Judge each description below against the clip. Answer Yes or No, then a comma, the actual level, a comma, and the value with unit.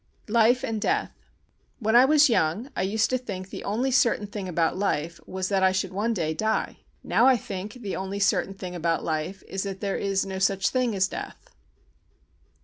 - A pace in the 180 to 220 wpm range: Yes, average, 200 wpm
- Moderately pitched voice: No, high, 195 Hz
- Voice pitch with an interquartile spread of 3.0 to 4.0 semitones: Yes, average, 3.3 semitones